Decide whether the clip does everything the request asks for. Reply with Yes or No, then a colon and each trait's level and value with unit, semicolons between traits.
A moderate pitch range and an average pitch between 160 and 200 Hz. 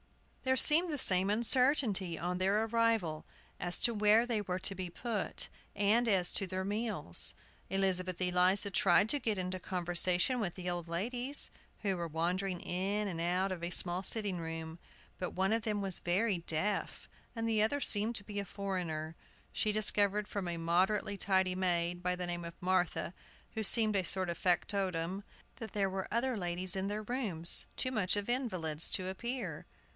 Yes: average, 3.3 semitones; high, 190 Hz